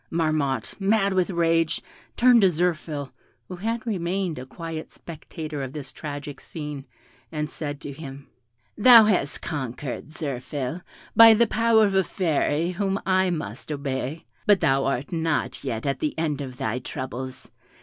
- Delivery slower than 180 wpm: Yes, average, 155 wpm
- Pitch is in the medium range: Yes, medium, 155 Hz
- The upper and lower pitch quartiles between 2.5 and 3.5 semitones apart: No, average, 5.1 semitones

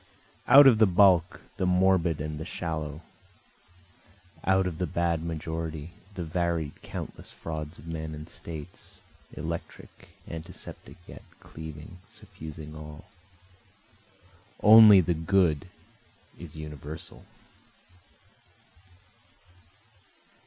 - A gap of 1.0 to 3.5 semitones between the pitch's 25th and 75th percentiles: Yes, average, 2.8 semitones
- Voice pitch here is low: Yes, very low, 80 Hz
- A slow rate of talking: Yes, slow, 95 wpm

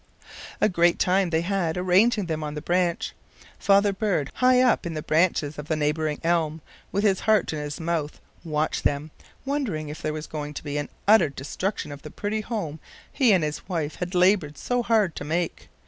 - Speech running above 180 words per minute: Yes, average, 195 wpm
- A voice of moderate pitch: Yes, medium, 170 Hz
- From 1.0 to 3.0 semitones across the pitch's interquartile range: No, average, 4.6 semitones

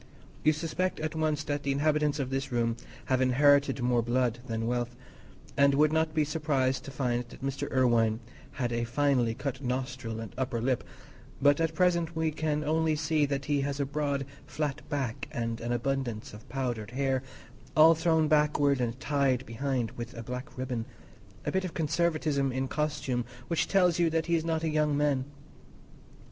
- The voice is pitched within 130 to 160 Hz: Yes, medium, 140 Hz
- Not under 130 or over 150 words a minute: No, average, 180 wpm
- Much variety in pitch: No, average, 3.7 semitones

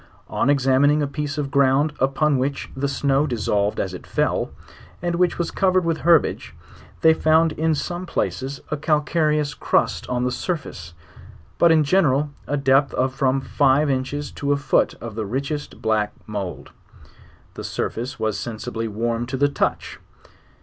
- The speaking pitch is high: No, medium, 140 Hz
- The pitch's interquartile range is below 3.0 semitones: No, average, 3.3 semitones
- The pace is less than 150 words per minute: No, average, 165 wpm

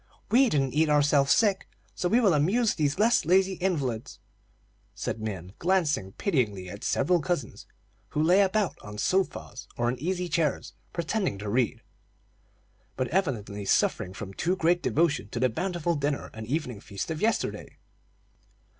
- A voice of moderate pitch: Yes, medium, 150 Hz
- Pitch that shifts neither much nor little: No, wide, 7.6 semitones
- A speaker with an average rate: Yes, average, 150 wpm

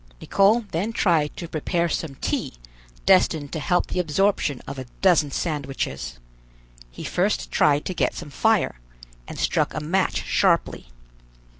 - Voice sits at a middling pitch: Yes, medium, 165 Hz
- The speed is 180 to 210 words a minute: No, average, 145 wpm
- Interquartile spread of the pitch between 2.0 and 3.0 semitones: No, average, 4.5 semitones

